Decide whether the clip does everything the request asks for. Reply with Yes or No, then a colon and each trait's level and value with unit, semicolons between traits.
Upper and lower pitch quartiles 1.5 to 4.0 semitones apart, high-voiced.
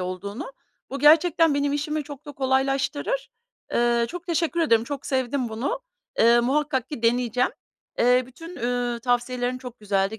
Yes: average, 3.6 semitones; very high, 260 Hz